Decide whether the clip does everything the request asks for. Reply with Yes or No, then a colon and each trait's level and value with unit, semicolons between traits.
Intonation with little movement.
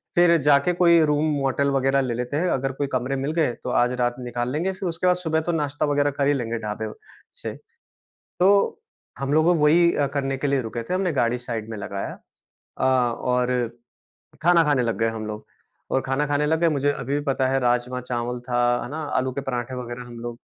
No: average, 3.9 semitones